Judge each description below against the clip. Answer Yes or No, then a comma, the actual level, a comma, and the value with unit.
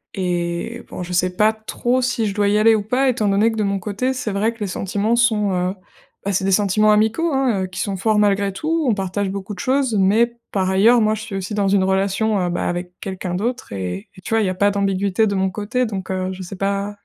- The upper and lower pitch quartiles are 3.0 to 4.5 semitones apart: No, narrow, 2.6 semitones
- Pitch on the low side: No, high, 200 Hz